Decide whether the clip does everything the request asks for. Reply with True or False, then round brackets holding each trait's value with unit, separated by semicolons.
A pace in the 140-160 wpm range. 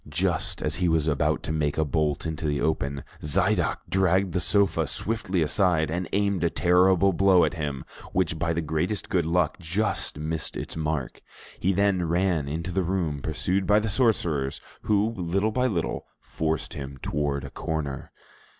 False (175 wpm)